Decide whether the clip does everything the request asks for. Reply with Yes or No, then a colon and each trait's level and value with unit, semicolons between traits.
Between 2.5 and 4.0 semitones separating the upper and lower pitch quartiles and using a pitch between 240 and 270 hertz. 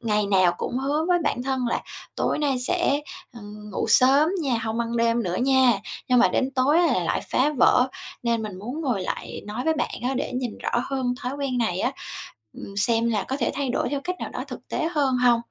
Yes: average, 2.9 semitones; very high, 250 Hz